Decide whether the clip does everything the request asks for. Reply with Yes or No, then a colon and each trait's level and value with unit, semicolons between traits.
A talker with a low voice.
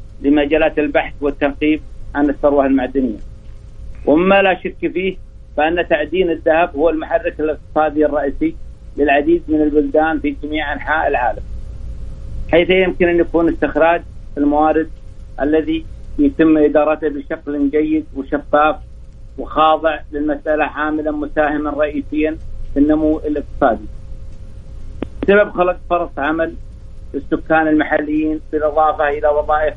No: medium, 150 Hz